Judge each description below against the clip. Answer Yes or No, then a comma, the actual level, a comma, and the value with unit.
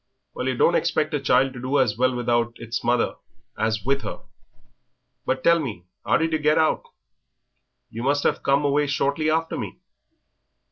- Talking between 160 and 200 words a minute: Yes, average, 180 wpm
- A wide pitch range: No, average, 3.6 semitones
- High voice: No, low, 135 Hz